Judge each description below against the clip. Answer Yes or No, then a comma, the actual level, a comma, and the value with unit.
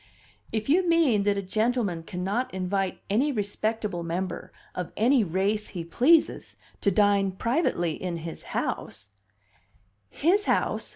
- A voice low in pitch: No, high, 200 Hz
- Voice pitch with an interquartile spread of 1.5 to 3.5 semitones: No, average, 5.0 semitones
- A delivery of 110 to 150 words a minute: Yes, slow, 135 wpm